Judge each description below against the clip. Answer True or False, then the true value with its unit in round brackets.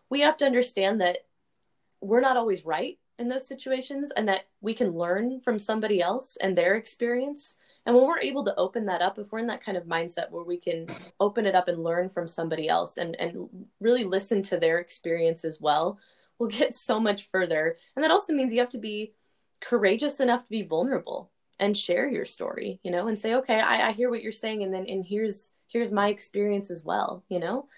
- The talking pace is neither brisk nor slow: False (220 wpm)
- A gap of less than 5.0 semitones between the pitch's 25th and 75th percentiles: False (5.3 semitones)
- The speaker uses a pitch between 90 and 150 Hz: False (215 Hz)